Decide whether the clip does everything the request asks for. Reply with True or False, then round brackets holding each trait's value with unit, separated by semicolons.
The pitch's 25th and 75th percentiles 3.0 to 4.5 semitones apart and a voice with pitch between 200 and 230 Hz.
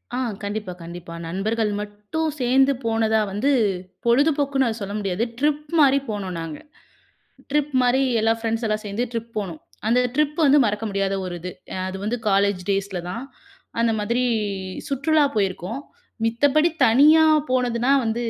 False (5.0 semitones; 225 Hz)